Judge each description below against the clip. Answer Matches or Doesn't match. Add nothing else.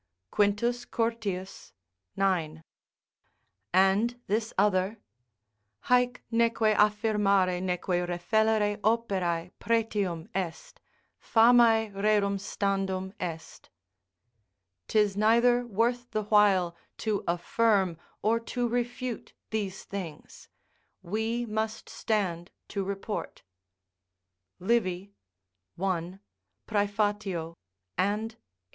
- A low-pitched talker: Doesn't match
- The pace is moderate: Doesn't match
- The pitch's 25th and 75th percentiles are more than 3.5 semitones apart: Doesn't match